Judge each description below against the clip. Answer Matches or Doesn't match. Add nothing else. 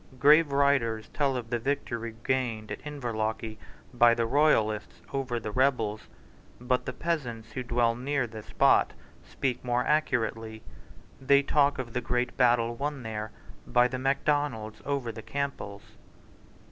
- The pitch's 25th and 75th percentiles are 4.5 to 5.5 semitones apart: Doesn't match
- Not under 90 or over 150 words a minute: Matches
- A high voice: Doesn't match